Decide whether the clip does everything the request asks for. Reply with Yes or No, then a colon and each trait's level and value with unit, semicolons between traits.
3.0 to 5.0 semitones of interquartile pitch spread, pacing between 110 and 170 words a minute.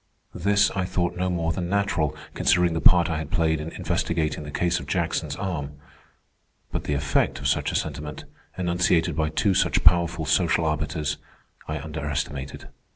No: narrow, 2.6 semitones; average, 165 wpm